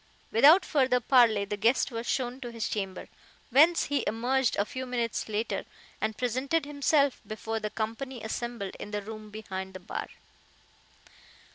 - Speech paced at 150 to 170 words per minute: Yes, average, 155 wpm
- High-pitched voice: Yes, high, 235 Hz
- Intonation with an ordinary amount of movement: Yes, average, 3.5 semitones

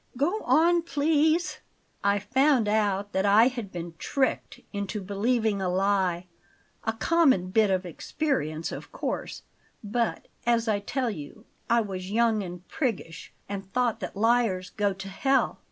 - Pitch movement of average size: Yes, average, 4.6 semitones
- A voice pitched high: Yes, high, 210 Hz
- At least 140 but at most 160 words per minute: Yes, average, 150 wpm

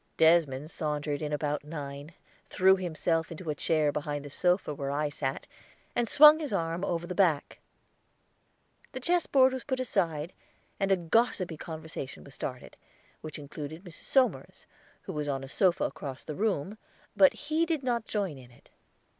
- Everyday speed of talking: Yes, average, 165 wpm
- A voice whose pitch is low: No, medium, 165 Hz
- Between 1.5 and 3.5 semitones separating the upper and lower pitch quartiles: No, average, 5.2 semitones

